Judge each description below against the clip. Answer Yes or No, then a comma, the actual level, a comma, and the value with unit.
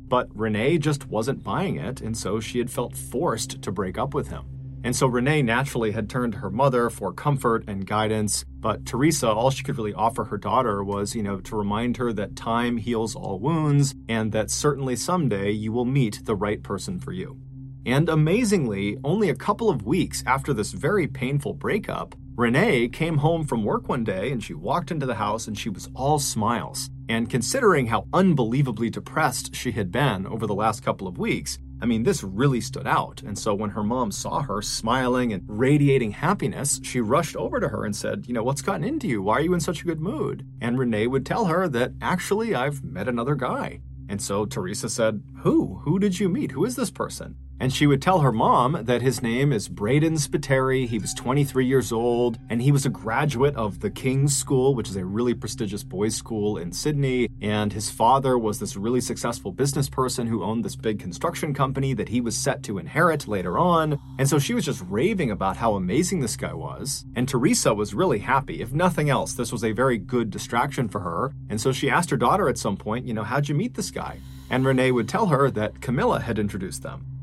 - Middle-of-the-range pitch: No, low, 125 Hz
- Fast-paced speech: Yes, fast, 220 wpm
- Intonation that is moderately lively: Yes, average, 4.1 semitones